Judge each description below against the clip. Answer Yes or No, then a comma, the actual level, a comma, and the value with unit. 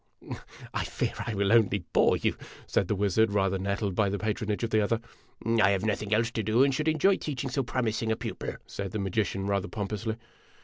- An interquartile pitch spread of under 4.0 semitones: Yes, narrow, 2.5 semitones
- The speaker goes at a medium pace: No, fast, 230 wpm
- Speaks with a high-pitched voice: No, low, 110 Hz